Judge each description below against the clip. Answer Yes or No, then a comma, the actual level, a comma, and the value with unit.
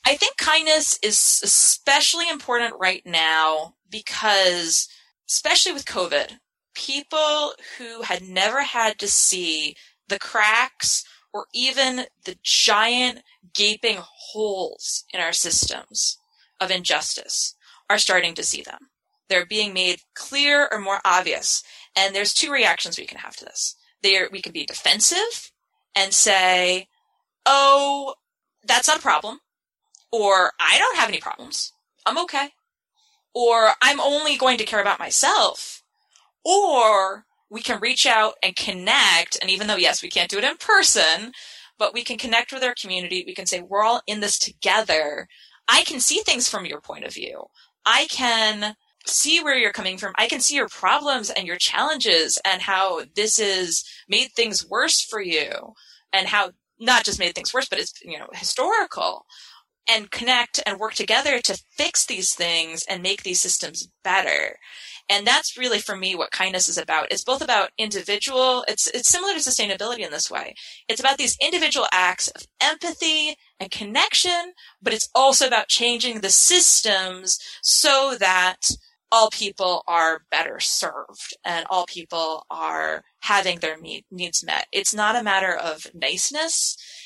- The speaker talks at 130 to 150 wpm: No, average, 160 wpm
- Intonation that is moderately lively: No, wide, 6.9 semitones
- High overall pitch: Yes, high, 220 Hz